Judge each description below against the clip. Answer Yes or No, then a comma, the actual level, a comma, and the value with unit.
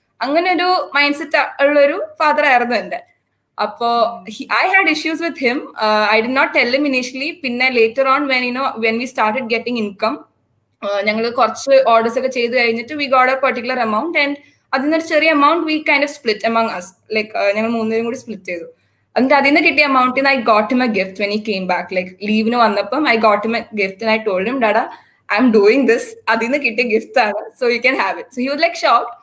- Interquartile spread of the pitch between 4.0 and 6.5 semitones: Yes, average, 4.4 semitones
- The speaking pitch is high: Yes, high, 245 Hz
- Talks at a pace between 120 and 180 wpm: No, average, 195 wpm